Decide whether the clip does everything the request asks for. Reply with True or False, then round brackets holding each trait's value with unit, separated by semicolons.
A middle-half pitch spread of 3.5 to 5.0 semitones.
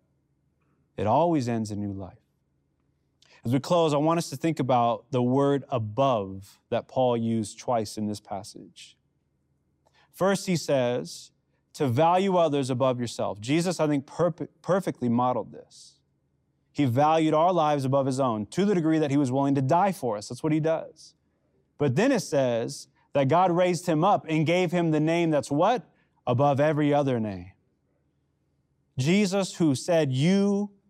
False (5.4 semitones)